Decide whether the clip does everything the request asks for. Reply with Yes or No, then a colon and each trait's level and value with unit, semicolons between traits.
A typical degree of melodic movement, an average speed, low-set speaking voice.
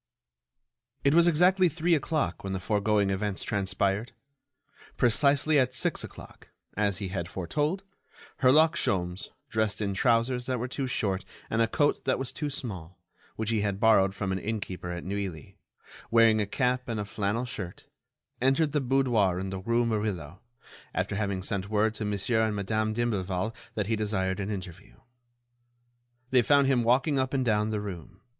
Yes: average, 4.6 semitones; average, 170 wpm; low, 110 Hz